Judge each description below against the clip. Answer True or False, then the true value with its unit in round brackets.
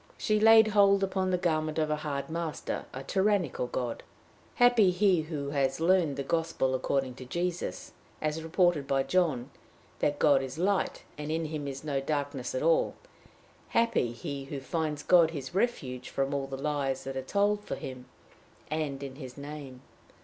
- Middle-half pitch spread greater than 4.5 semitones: True (4.9 semitones)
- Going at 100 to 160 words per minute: False (175 wpm)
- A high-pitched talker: False (150 Hz)